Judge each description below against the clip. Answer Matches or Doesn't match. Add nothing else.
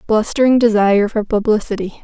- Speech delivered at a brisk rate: Doesn't match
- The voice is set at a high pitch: Matches